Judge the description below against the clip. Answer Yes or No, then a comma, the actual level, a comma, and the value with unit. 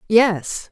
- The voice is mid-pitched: No, high, 205 Hz